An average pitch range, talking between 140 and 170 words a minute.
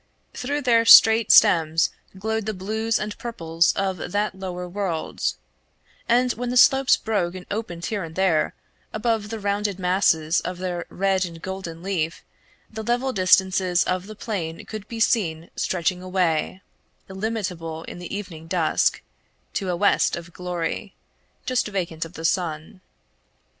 Yes: average, 3.9 semitones; average, 150 wpm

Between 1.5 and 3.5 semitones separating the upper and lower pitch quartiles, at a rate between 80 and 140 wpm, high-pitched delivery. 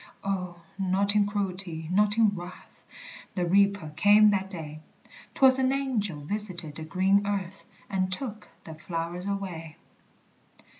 Yes: average, 2.9 semitones; slow, 135 wpm; high, 195 Hz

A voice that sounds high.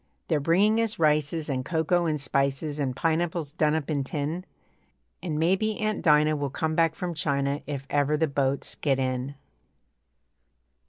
No: medium, 150 Hz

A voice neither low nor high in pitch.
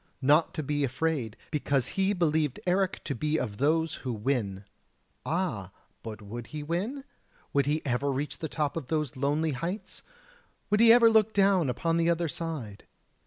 Yes: medium, 150 Hz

